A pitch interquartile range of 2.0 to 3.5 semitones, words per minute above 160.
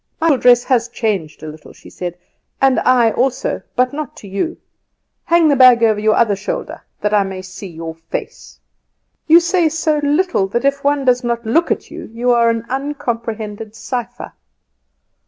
No: average, 5.1 semitones; average, 175 wpm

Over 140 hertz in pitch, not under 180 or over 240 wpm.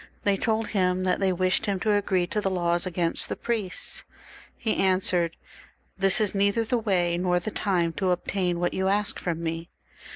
Yes: medium, 185 Hz; average, 195 wpm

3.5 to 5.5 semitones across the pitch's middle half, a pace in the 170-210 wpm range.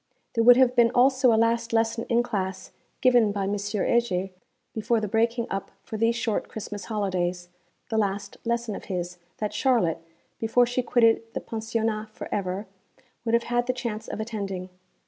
No: average, 2.7 semitones; average, 175 wpm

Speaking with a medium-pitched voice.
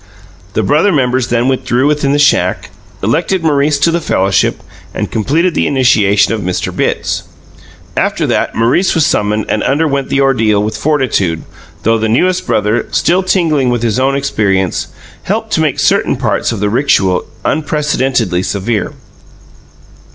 No: low, 130 Hz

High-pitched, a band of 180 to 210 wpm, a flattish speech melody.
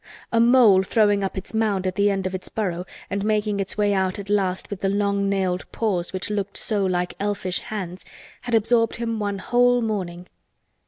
Yes: high, 200 Hz; average, 200 wpm; narrow, 2.3 semitones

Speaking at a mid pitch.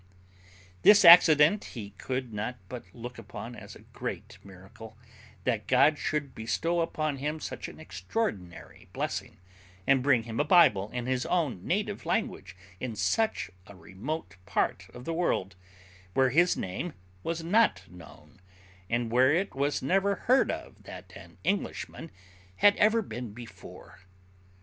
No: low, 130 Hz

